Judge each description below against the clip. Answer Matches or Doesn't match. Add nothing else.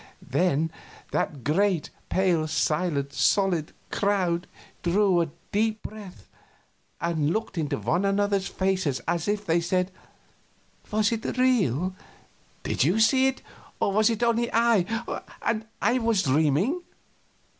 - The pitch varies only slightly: Doesn't match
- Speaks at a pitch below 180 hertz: Doesn't match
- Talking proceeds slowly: Matches